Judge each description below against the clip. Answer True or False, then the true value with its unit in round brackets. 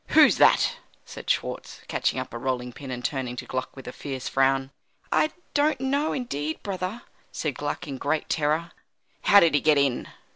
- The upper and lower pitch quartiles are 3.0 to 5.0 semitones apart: False (5.6 semitones)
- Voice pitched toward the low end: False (145 Hz)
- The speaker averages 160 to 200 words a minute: True (185 wpm)